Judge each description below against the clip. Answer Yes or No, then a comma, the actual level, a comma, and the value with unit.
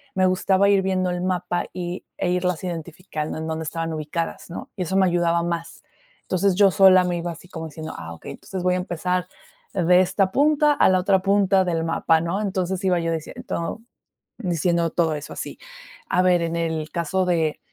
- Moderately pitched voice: Yes, medium, 180 Hz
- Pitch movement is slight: Yes, narrow, 2.1 semitones